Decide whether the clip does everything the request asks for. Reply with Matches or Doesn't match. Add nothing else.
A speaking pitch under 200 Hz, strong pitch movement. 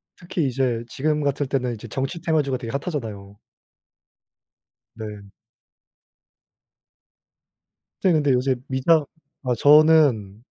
Doesn't match